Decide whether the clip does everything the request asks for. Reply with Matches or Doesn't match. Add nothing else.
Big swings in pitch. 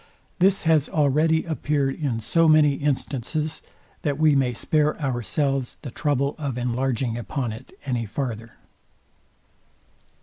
Doesn't match